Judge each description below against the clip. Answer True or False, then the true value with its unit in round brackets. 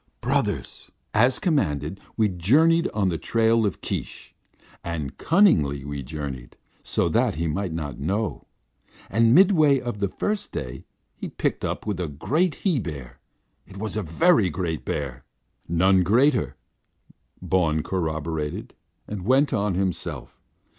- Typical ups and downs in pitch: False (7.5 semitones)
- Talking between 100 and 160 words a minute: True (140 wpm)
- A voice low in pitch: True (95 Hz)